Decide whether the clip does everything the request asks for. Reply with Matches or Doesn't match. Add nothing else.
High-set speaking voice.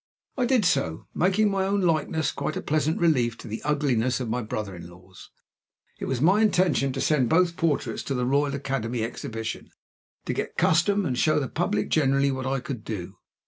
Doesn't match